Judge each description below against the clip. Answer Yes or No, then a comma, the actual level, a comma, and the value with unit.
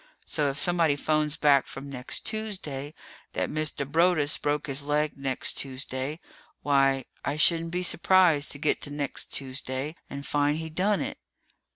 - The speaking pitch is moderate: Yes, medium, 145 Hz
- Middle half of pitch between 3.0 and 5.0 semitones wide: No, narrow, 2.5 semitones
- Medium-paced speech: Yes, average, 160 wpm